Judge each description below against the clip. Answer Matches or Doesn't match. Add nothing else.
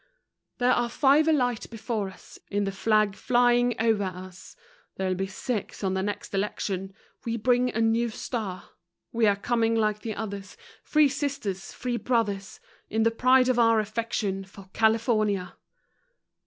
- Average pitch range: Matches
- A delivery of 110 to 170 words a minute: Matches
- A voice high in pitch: Matches